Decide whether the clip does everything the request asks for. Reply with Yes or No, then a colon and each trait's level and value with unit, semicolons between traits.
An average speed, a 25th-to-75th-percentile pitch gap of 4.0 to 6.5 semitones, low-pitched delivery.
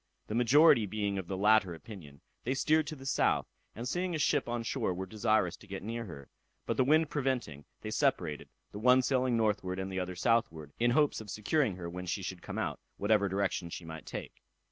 No: fast, 215 wpm; wide, 5.5 semitones; low, 110 Hz